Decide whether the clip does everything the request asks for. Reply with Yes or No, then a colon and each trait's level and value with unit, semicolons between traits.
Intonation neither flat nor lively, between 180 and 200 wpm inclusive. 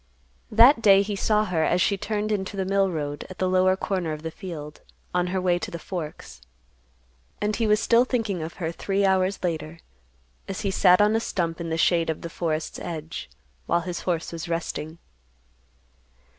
Yes: average, 3.2 semitones; average, 195 wpm